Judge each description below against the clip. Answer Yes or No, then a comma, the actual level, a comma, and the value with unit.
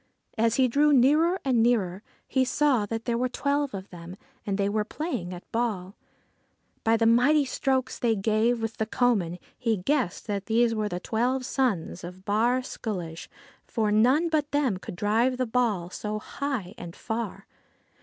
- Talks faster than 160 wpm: Yes, average, 175 wpm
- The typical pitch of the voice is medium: No, high, 225 Hz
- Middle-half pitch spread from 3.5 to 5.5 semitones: Yes, average, 4.2 semitones